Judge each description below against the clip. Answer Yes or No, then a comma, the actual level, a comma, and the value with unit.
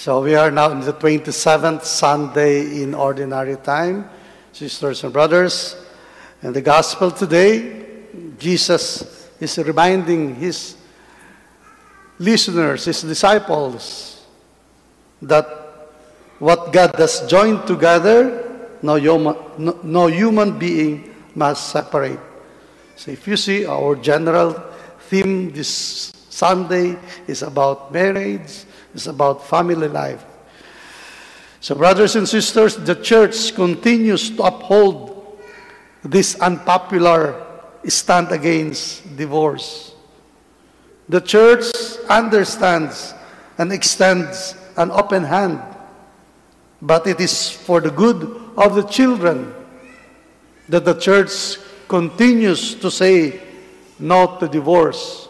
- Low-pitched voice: No, medium, 175 Hz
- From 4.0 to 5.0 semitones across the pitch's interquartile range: Yes, average, 4.3 semitones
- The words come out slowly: Yes, slow, 100 wpm